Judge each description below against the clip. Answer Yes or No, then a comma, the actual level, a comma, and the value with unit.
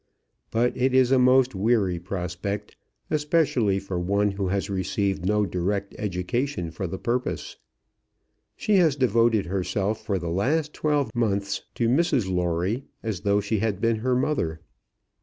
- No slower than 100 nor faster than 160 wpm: Yes, average, 150 wpm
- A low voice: Yes, low, 105 Hz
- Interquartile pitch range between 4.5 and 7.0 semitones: Yes, average, 4.8 semitones